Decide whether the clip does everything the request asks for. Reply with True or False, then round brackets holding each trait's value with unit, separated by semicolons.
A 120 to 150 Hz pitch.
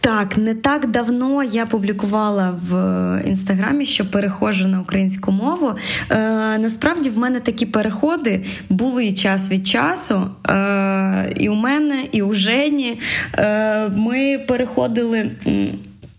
False (215 Hz)